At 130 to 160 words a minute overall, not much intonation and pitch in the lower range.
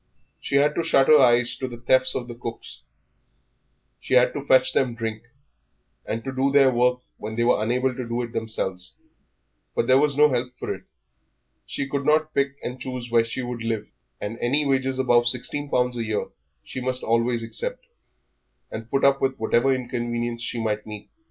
No: average, 190 wpm; narrow, 2.2 semitones; low, 125 Hz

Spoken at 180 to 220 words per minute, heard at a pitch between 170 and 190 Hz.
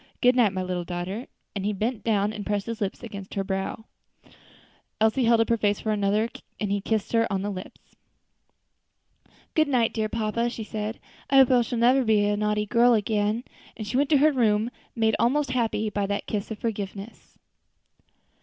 No: average, 190 wpm; high, 215 Hz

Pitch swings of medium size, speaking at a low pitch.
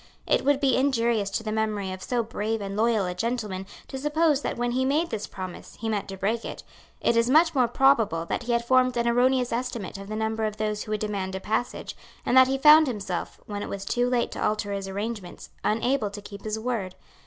No: average, 3.7 semitones; high, 225 Hz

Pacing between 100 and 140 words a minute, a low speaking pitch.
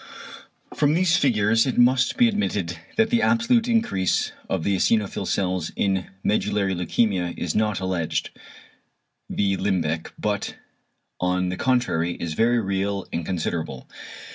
Yes: slow, 135 wpm; low, 100 Hz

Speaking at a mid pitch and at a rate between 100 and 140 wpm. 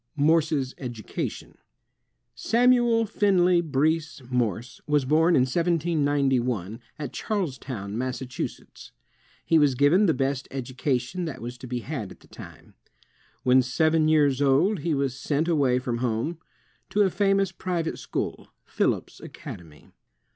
Yes: medium, 145 Hz; slow, 135 wpm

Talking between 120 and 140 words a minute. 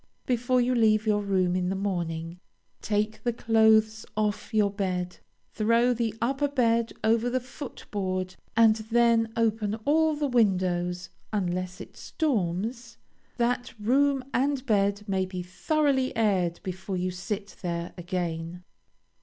Yes: slow, 135 wpm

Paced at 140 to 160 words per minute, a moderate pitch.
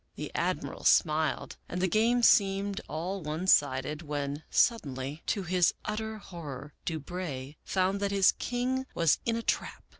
Yes: average, 155 wpm; medium, 180 Hz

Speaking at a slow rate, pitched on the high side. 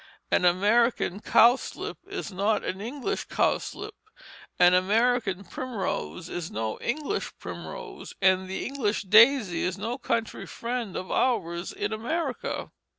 Yes: slow, 125 wpm; high, 215 Hz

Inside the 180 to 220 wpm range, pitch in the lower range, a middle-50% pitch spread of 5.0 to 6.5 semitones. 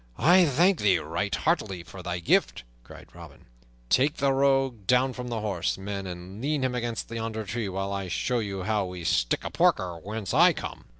Yes: average, 195 wpm; low, 105 Hz; average, 5.3 semitones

